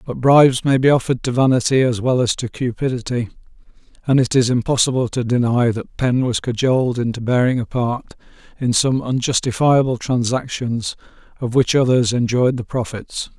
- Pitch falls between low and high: No, low, 125 Hz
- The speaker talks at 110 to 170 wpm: Yes, average, 160 wpm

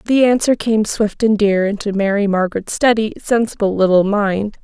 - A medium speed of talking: Yes, average, 170 wpm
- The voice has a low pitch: No, high, 210 Hz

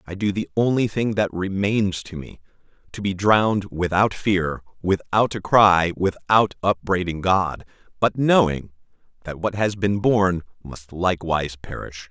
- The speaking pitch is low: Yes, very low, 95 Hz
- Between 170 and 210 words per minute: No, average, 145 wpm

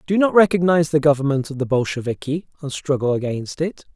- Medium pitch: Yes, medium, 150 Hz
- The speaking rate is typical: Yes, average, 180 wpm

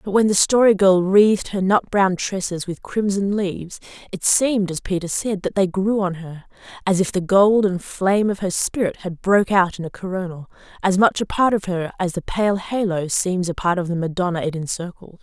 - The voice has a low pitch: No, high, 190 Hz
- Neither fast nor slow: No, fast, 215 wpm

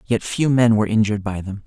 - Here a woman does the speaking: No, male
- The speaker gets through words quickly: Yes, fast, 250 wpm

